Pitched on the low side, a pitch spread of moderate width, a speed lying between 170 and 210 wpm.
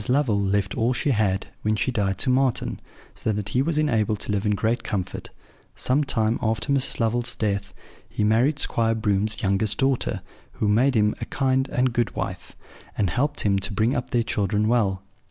Yes: low, 110 Hz; average, 3.6 semitones; average, 190 wpm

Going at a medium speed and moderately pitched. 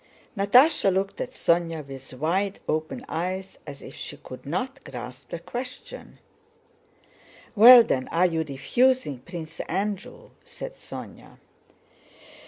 No: slow, 120 wpm; medium, 175 Hz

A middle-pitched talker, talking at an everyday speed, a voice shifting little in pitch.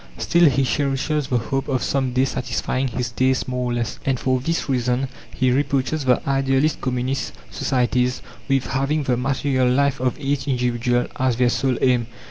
No: low, 130 Hz; average, 175 wpm; narrow, 1.6 semitones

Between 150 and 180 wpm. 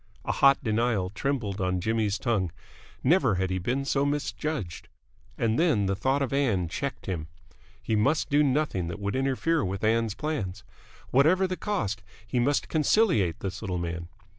Yes: average, 165 wpm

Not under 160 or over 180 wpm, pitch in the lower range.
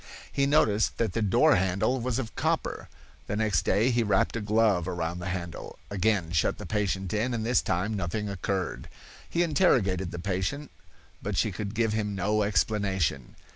Yes: average, 175 wpm; low, 105 Hz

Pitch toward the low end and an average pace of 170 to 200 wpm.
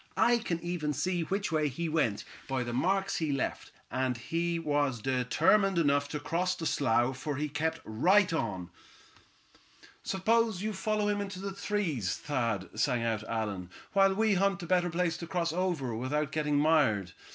No: medium, 160 Hz; average, 175 wpm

